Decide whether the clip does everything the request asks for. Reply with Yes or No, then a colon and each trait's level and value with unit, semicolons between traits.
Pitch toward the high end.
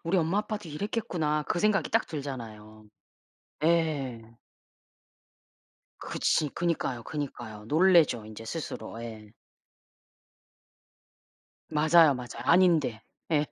No: medium, 150 Hz